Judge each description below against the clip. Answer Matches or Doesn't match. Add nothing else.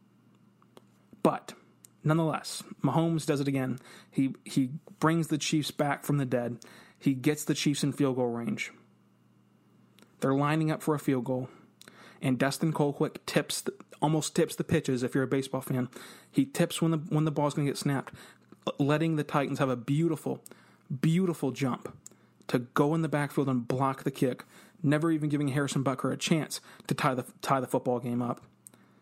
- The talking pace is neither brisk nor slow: Matches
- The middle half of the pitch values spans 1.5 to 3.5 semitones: Matches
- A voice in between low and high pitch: Matches